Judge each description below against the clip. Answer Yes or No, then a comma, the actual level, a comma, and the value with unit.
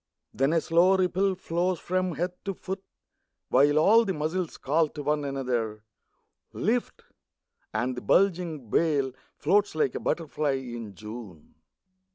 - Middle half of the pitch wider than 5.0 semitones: Yes, wide, 5.6 semitones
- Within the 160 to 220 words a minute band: No, average, 145 wpm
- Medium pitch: Yes, medium, 155 Hz